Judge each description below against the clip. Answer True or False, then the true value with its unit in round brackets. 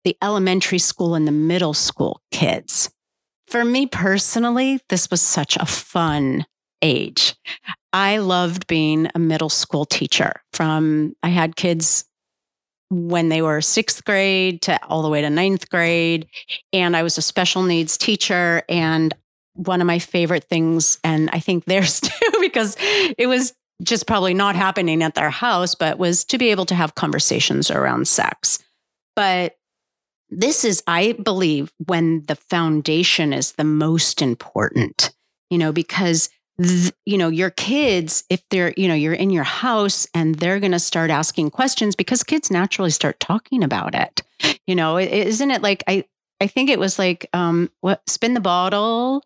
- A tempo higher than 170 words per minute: False (165 wpm)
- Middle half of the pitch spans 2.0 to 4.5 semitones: True (3.3 semitones)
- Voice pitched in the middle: True (180 Hz)